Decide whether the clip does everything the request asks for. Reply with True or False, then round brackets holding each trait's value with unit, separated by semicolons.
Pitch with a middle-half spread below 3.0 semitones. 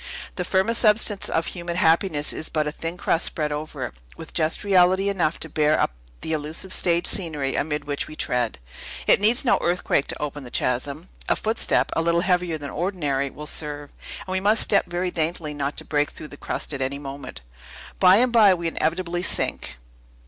False (3.9 semitones)